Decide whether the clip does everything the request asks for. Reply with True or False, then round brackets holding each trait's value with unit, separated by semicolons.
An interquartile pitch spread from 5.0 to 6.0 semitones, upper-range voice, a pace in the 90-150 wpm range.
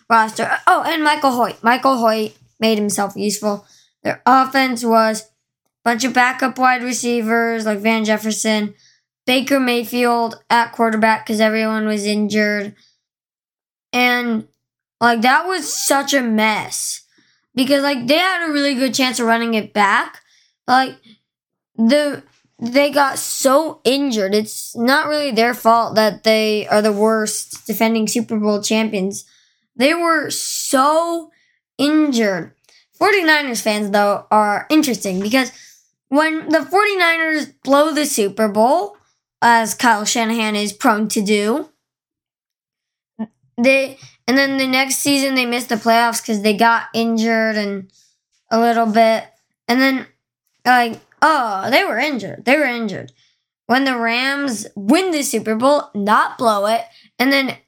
False (3.8 semitones; 235 Hz; 140 wpm)